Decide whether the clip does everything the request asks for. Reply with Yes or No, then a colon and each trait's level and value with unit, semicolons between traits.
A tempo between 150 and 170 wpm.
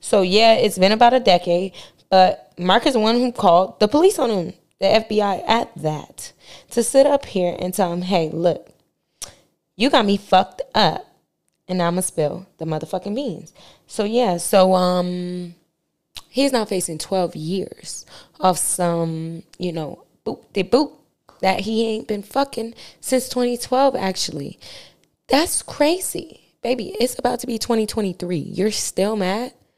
Yes: average, 165 wpm